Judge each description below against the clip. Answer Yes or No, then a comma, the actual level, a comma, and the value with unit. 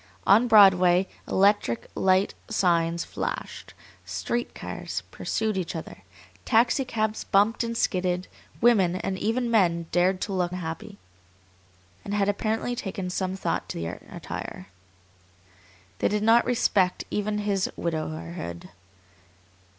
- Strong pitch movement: No, average, 3.4 semitones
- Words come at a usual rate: No, slow, 120 wpm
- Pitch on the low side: No, high, 195 Hz